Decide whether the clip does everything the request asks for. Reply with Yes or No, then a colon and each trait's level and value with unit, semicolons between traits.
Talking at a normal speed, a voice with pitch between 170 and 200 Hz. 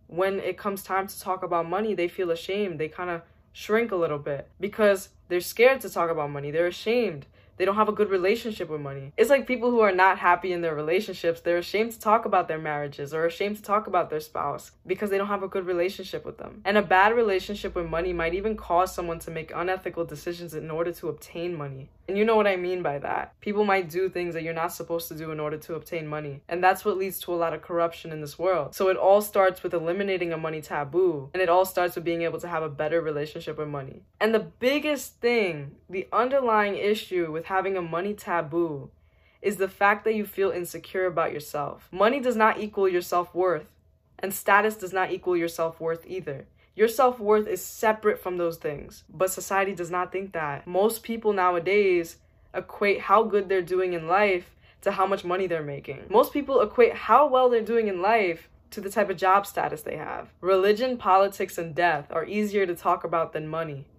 No: fast, 225 wpm; medium, 185 Hz